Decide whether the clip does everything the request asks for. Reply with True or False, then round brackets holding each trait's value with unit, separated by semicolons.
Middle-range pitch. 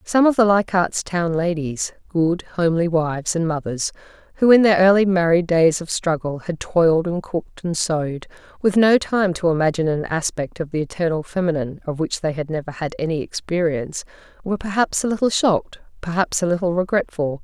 True (170 Hz)